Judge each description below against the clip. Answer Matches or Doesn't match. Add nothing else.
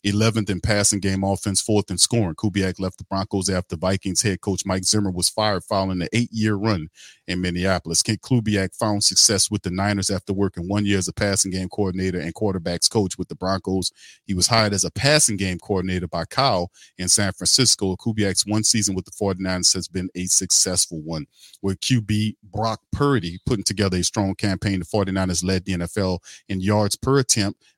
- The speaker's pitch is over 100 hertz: Doesn't match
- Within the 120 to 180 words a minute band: Doesn't match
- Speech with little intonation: Matches